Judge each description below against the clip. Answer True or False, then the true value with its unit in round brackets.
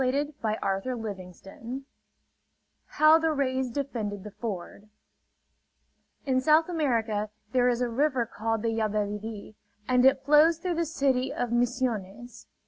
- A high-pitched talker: True (245 Hz)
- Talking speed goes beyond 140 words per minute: False (135 wpm)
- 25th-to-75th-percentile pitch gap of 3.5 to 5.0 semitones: True (4.2 semitones)